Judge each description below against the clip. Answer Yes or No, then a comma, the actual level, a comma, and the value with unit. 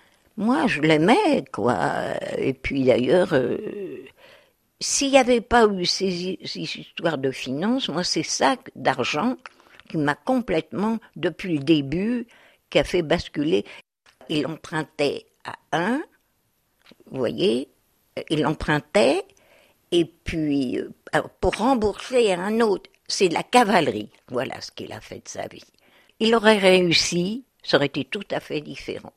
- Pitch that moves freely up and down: Yes, wide, 7.8 semitones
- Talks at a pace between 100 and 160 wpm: Yes, slow, 145 wpm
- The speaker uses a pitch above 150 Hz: Yes, medium, 185 Hz